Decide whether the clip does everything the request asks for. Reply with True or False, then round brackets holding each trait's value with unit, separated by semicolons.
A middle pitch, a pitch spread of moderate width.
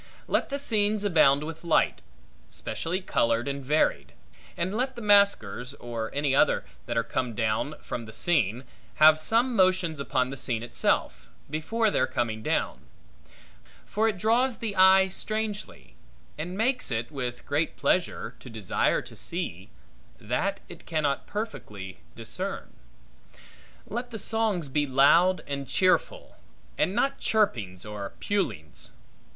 False (155 Hz; 8.9 semitones)